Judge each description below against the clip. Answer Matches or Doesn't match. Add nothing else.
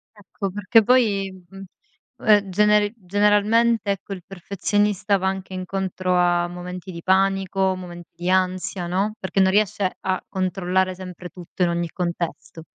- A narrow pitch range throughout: Matches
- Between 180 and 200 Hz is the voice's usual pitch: Matches